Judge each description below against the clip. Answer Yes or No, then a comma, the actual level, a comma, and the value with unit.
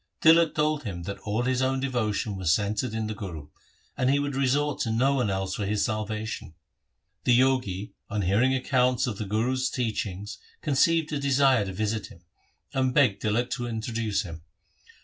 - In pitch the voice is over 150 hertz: No, low, 115 Hz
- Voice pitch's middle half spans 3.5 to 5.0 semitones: Yes, average, 4.2 semitones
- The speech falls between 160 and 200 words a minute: Yes, average, 180 wpm